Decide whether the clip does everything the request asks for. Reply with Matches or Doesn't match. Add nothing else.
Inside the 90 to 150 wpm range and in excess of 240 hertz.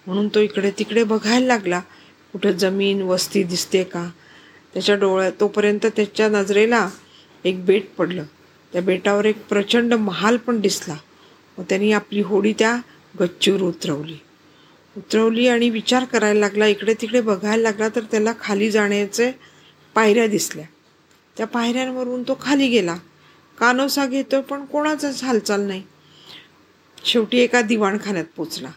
Doesn't match